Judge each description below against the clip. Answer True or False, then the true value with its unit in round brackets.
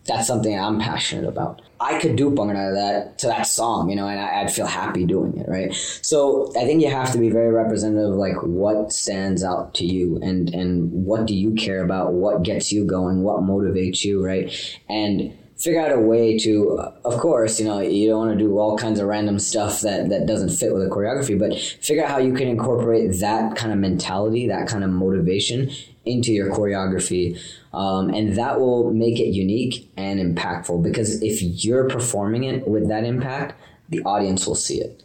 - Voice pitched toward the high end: False (105 Hz)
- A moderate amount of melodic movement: True (3.3 semitones)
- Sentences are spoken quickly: True (210 wpm)